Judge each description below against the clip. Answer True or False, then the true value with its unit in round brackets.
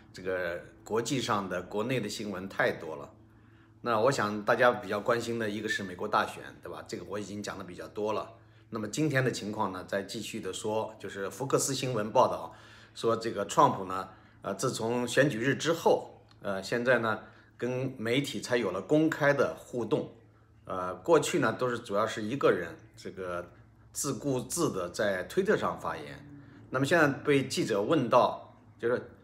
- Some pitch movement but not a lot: True (3.0 semitones)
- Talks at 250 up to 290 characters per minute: True (265 characters per minute)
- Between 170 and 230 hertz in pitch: False (110 Hz)